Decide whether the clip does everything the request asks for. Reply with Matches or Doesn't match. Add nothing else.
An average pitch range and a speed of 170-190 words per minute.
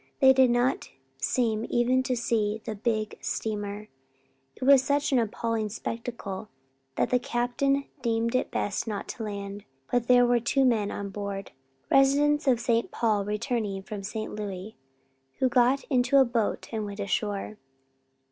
Doesn't match